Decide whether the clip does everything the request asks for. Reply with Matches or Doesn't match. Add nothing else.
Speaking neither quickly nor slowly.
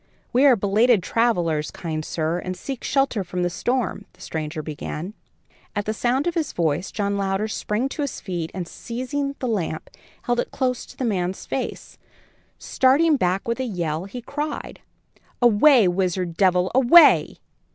Matches